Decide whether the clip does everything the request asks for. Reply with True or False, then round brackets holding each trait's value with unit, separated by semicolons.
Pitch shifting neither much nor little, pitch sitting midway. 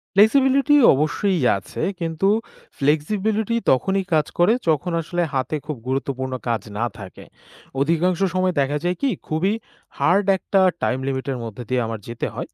False (6.4 semitones; 160 Hz)